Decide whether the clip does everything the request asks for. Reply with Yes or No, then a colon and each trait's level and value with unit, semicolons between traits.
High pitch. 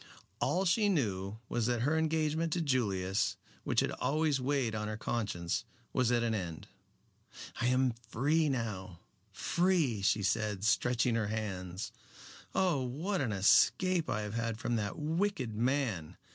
No: low, 120 Hz